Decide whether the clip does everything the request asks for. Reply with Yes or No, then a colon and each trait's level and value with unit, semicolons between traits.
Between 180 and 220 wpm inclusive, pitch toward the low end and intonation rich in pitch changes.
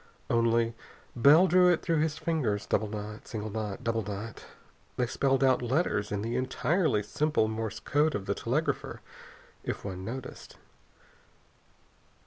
No: average, 140 wpm; low, 115 Hz; wide, 5.9 semitones